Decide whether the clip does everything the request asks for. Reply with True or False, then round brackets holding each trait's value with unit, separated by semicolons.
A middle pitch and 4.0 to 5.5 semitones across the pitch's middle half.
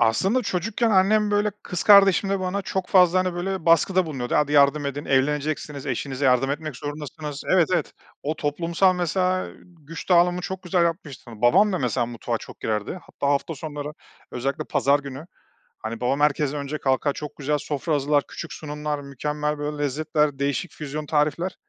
True (150 Hz; 4.3 semitones)